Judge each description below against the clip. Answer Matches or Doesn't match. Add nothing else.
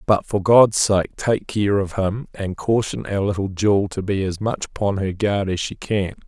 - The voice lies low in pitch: Matches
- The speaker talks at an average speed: Doesn't match